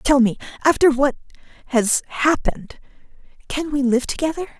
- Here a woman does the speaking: Yes, female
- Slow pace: Yes, slow, 130 wpm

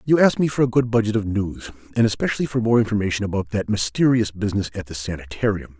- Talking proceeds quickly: Yes, fast, 220 wpm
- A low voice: Yes, low, 105 Hz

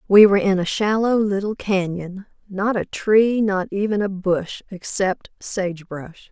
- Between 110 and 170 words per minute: Yes, average, 150 wpm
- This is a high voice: Yes, high, 195 Hz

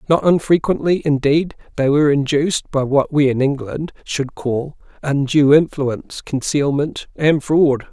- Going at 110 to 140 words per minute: Yes, slow, 135 wpm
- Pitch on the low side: No, medium, 145 Hz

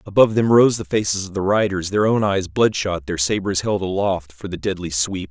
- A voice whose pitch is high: No, very low, 95 Hz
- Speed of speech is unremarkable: No, fast, 225 wpm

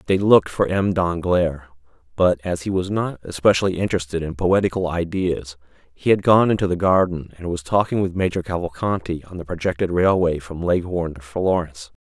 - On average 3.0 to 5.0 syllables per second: No, 5.5 syllables/s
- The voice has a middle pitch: No, very low, 90 Hz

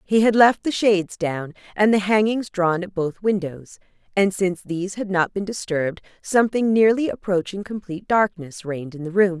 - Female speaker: Yes, female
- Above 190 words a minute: No, average, 185 wpm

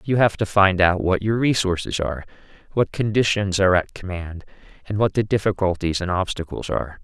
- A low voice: Yes, very low, 95 Hz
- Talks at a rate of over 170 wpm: Yes, average, 180 wpm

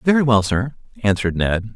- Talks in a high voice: No, low, 115 Hz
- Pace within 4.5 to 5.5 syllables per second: No, 5.7 syllables/s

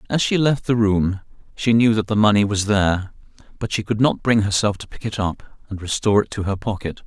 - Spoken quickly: Yes, fast, 240 wpm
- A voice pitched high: No, low, 105 Hz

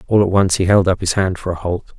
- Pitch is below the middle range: Yes, very low, 95 Hz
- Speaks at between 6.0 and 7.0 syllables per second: Yes, 6.4 syllables/s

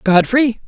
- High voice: Yes, high, 225 Hz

